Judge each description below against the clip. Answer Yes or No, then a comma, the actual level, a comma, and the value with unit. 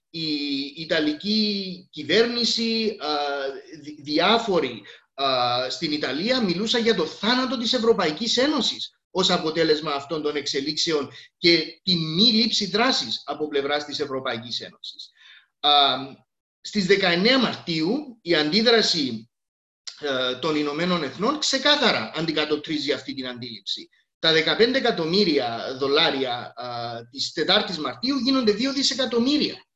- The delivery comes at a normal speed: No, slow, 105 wpm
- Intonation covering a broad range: Yes, wide, 7.7 semitones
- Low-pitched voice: No, medium, 165 Hz